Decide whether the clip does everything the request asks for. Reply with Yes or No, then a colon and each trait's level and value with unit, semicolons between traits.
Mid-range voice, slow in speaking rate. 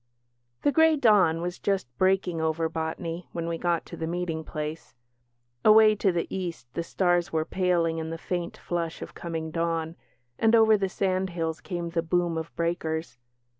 No: medium, 170 Hz; average, 170 wpm